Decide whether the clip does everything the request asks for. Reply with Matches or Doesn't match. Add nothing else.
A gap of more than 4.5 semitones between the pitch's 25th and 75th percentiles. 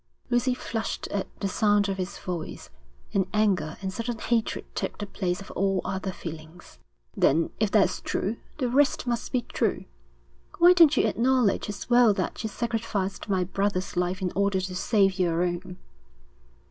Doesn't match